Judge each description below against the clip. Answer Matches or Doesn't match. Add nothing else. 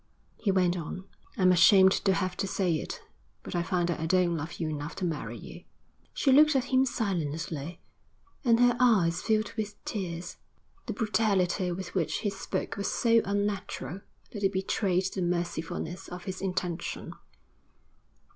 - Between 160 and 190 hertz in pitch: Matches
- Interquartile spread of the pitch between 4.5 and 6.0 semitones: Doesn't match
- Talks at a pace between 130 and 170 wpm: Matches